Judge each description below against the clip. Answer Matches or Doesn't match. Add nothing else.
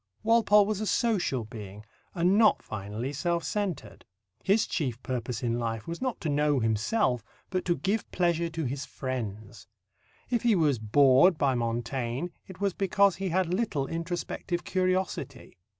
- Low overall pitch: Doesn't match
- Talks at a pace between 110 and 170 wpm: Matches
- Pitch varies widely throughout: Matches